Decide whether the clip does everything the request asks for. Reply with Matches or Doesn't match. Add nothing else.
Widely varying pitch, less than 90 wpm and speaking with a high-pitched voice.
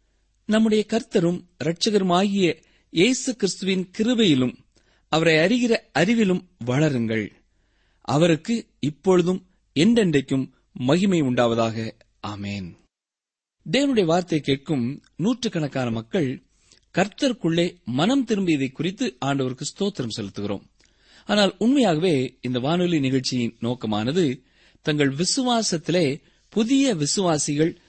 Doesn't match